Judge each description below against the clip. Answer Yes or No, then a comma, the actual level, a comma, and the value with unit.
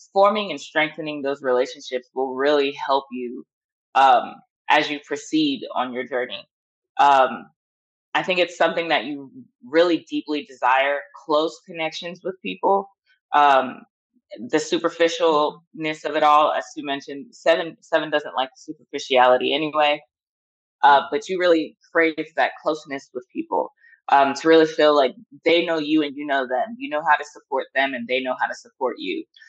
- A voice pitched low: No, medium, 150 Hz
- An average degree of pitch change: Yes, average, 3.7 semitones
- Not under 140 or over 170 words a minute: Yes, average, 160 wpm